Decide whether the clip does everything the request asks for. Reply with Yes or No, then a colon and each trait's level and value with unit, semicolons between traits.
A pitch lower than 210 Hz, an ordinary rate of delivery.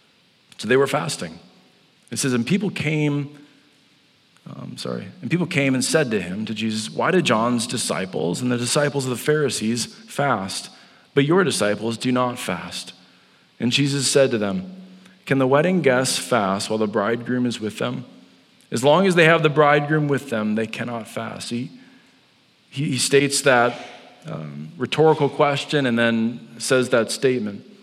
Yes: low, 135 Hz; average, 170 wpm